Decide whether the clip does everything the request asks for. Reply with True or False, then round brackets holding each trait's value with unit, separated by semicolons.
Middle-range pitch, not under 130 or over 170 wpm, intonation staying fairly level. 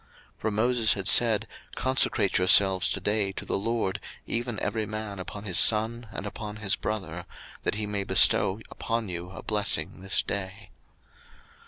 False (105 Hz; 160 wpm; 2.3 semitones)